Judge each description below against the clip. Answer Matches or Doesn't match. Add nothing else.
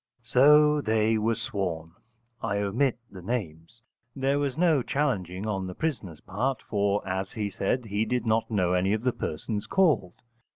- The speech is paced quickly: Doesn't match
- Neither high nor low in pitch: Doesn't match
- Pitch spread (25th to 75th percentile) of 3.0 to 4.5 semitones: Doesn't match